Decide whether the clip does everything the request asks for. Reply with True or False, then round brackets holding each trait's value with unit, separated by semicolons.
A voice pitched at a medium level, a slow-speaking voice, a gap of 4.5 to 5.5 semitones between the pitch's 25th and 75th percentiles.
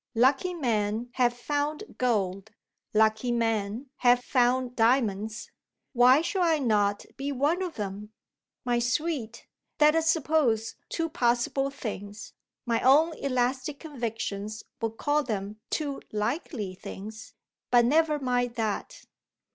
False (245 Hz; 125 wpm; 4.8 semitones)